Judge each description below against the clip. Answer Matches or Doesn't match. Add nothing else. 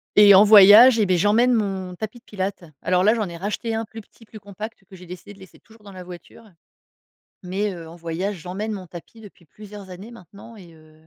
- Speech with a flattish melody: Doesn't match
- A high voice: Matches